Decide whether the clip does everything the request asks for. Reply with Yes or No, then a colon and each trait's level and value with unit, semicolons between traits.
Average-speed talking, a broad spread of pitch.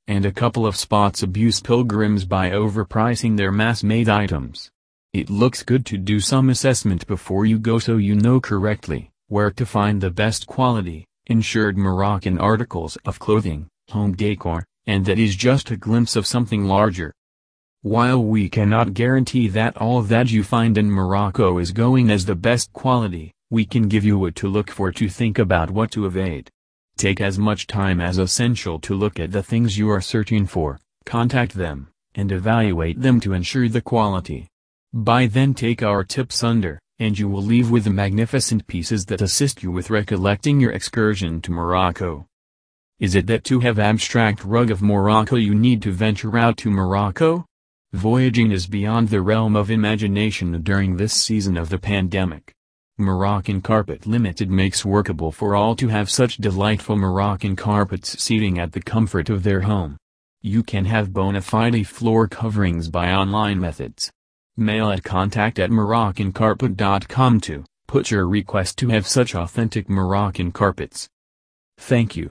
No: average, 170 wpm; average, 3.0 semitones